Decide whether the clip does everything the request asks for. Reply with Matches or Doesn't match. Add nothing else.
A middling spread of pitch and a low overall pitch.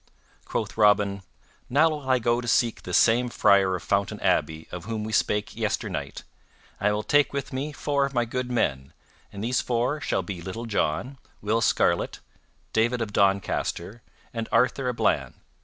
Matches